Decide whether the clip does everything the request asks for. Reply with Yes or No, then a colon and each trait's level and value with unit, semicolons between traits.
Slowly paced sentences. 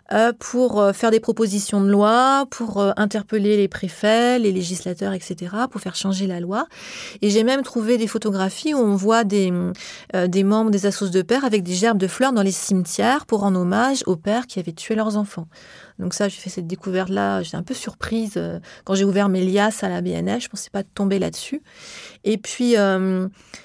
No: average, 215 wpm